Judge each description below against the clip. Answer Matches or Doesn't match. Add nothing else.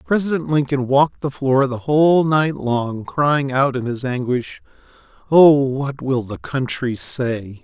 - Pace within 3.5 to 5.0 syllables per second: Matches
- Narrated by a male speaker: Matches